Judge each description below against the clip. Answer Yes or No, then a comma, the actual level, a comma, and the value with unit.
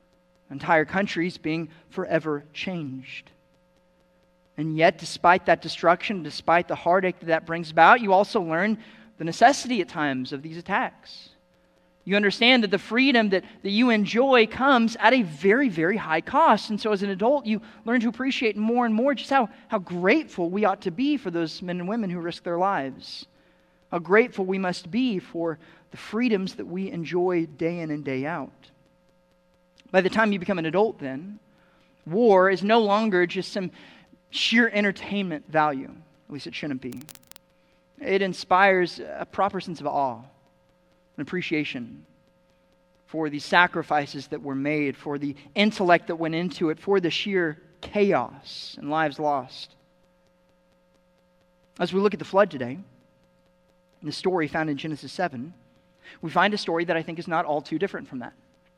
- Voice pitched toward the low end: No, medium, 180 Hz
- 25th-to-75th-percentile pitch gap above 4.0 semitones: Yes, average, 4.5 semitones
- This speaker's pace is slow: No, average, 170 wpm